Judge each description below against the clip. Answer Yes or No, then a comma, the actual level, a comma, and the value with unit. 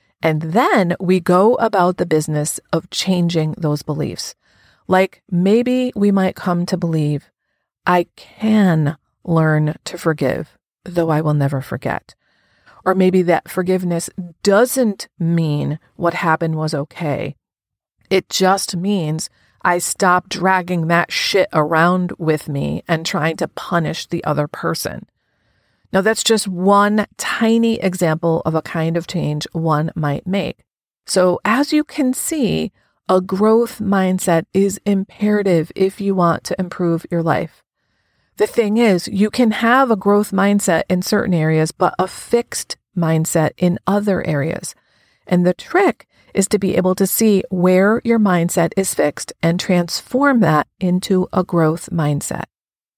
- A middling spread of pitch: Yes, average, 3.6 semitones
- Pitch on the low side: No, medium, 180 Hz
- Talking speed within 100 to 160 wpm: Yes, average, 145 wpm